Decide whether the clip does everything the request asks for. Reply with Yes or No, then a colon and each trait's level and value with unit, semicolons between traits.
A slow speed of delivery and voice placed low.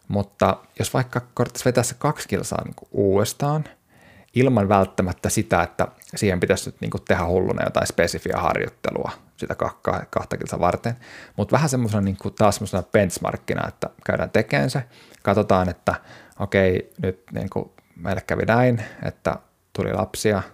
No: average, 145 wpm; low, 105 Hz